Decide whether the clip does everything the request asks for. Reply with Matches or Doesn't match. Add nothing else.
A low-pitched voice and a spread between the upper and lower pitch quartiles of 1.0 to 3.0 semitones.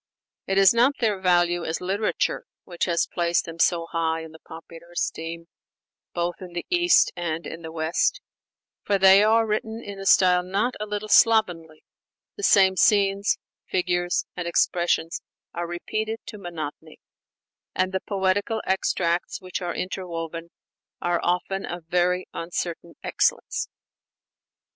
Doesn't match